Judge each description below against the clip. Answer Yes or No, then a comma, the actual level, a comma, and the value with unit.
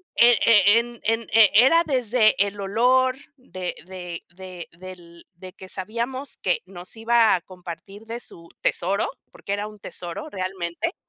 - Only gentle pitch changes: No, average, 4.2 semitones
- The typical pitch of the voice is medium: No, high, 205 Hz